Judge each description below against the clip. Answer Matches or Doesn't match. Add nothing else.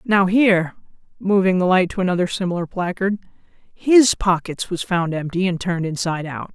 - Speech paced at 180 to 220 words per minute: Doesn't match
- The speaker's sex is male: Doesn't match